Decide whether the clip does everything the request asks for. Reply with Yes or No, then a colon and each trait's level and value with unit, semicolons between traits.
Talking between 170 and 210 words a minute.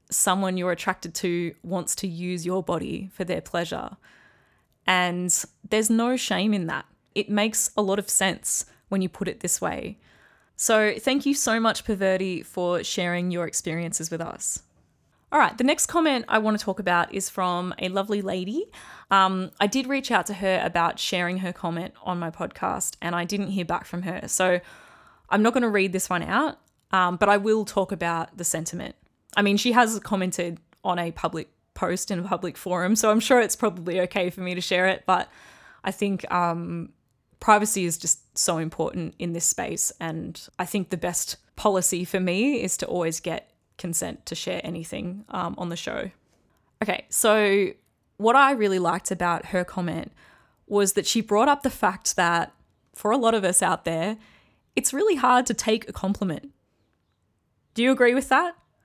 Yes: average, 190 wpm